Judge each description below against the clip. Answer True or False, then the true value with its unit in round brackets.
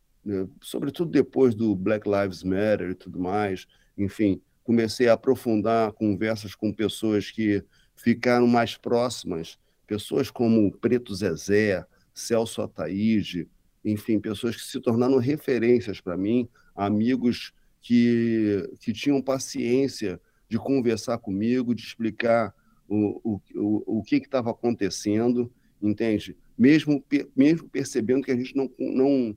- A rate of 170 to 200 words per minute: False (125 wpm)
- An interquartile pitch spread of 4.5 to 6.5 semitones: False (3.0 semitones)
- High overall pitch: False (110 Hz)